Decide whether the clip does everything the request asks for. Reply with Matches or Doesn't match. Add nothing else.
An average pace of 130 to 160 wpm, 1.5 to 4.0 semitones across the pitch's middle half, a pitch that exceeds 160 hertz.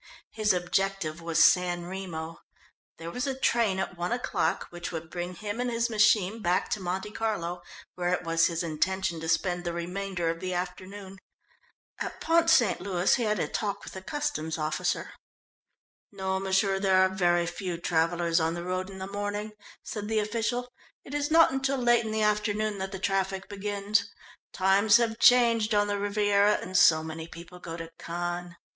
Doesn't match